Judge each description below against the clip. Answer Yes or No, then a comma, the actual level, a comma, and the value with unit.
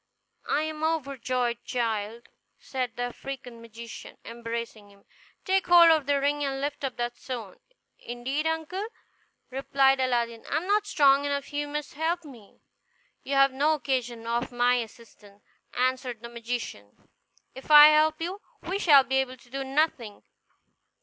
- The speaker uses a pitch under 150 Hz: No, very high, 265 Hz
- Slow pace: No, average, 155 wpm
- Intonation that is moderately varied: Yes, average, 4.0 semitones